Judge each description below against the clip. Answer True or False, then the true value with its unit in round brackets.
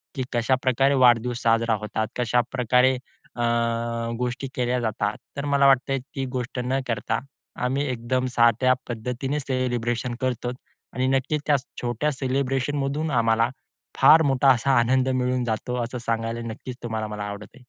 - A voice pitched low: True (125 Hz)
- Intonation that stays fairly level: True (2.2 semitones)